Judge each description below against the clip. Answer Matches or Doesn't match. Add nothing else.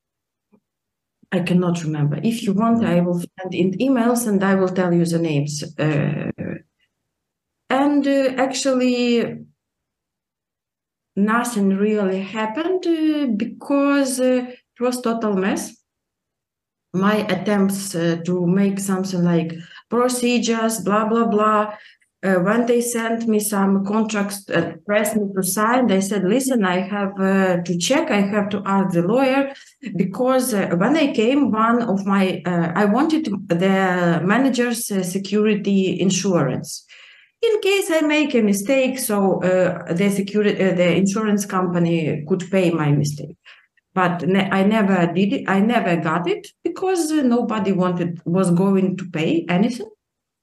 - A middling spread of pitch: Matches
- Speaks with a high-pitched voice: Matches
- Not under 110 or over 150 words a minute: Matches